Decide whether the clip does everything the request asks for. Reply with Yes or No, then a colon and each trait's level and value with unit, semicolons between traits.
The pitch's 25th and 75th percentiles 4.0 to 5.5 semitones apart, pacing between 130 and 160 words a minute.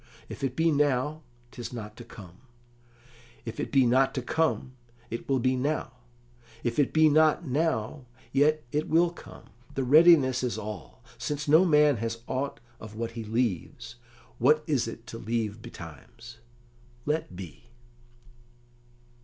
Yes: average, 4.6 semitones; average, 150 wpm